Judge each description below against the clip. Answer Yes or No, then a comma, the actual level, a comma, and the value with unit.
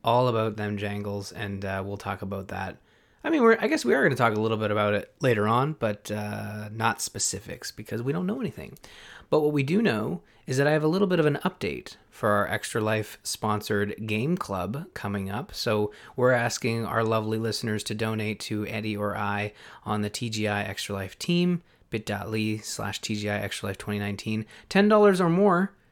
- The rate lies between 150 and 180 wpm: No, average, 200 wpm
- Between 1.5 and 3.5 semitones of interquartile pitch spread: Yes, average, 3.0 semitones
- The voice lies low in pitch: Yes, low, 110 Hz